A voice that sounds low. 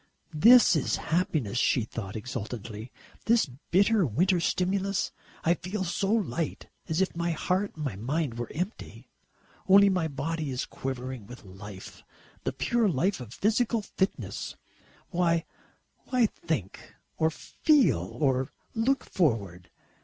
No: medium, 165 Hz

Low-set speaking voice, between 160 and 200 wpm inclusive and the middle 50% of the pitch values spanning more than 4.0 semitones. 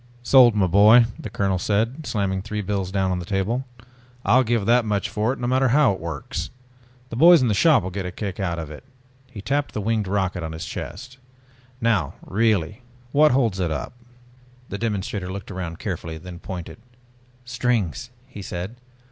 Yes: low, 105 Hz; average, 190 wpm; average, 4.5 semitones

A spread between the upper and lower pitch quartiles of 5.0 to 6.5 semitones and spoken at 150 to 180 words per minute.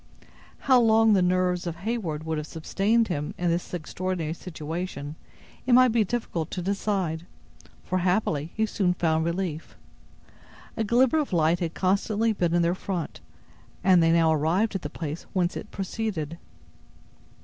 No: average, 4.2 semitones; average, 160 wpm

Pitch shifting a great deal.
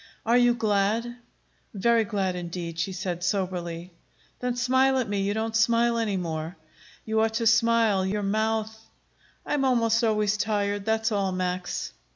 No: average, 3.4 semitones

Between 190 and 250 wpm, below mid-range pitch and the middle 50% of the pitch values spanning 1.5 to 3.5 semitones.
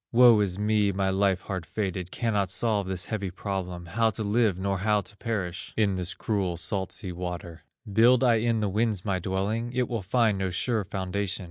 Yes: average, 200 wpm; low, 100 Hz; average, 2.9 semitones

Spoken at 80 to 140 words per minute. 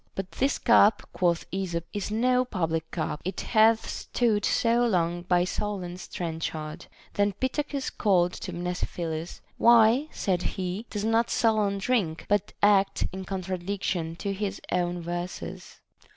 Yes: slow, 135 wpm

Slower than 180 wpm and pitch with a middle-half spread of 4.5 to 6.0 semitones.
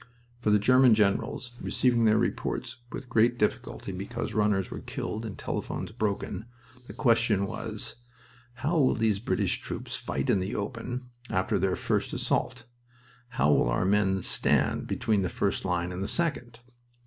No: average, 160 wpm; average, 3.7 semitones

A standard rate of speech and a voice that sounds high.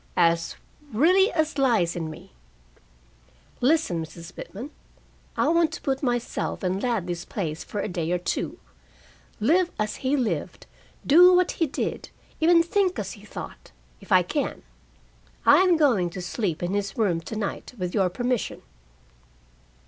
Yes: average, 155 wpm; high, 220 Hz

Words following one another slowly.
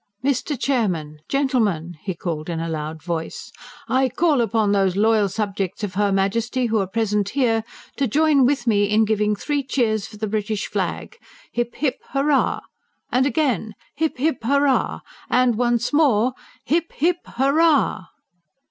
No: average, 155 wpm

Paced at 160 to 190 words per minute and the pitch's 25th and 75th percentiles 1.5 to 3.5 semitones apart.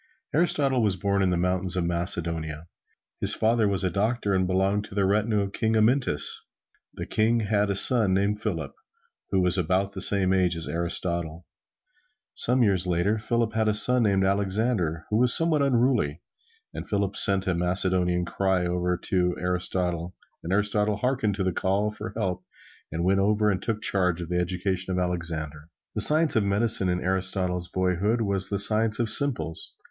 Yes: average, 180 wpm; average, 3.1 semitones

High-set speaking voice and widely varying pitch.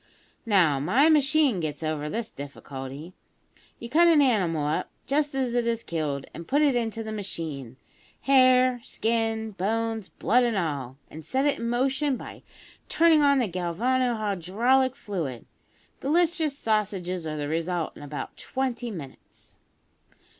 Yes: high, 220 Hz; wide, 8.0 semitones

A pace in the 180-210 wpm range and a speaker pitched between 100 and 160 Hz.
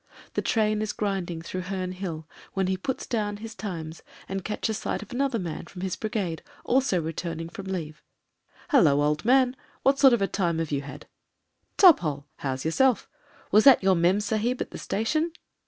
No: average, 190 wpm; high, 195 Hz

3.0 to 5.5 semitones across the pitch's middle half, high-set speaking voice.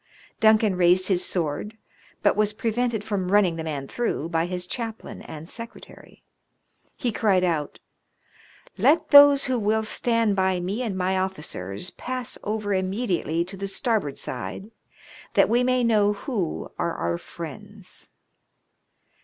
Yes: average, 4.3 semitones; high, 200 Hz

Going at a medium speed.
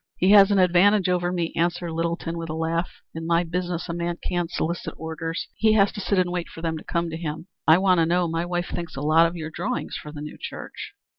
No: fast, 250 wpm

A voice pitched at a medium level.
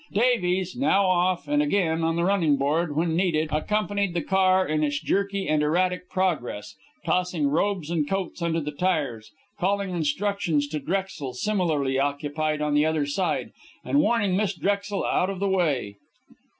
Yes: medium, 175 Hz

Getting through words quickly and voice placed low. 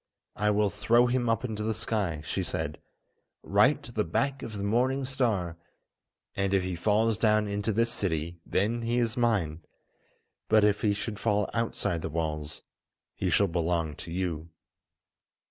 No: average, 165 wpm; low, 105 Hz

